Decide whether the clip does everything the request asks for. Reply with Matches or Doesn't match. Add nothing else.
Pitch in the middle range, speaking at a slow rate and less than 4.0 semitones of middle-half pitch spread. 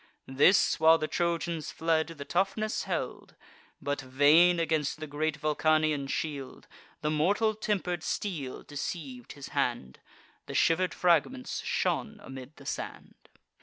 Matches